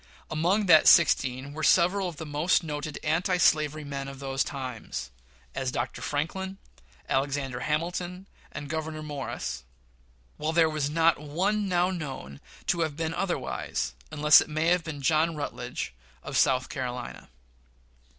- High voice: No, medium, 155 Hz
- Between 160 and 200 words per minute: No, average, 140 wpm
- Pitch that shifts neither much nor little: Yes, average, 3.4 semitones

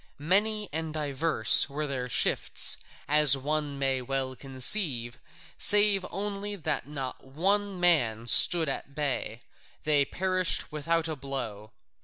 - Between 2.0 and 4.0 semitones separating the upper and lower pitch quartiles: No, average, 4.9 semitones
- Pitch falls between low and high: Yes, medium, 150 Hz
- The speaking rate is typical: No, slow, 125 wpm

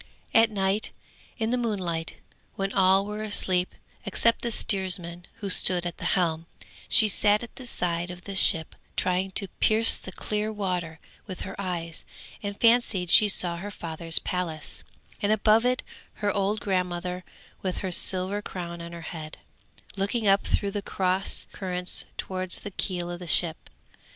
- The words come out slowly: No, average, 165 wpm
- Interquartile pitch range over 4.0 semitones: No, average, 2.8 semitones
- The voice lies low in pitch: No, high, 190 Hz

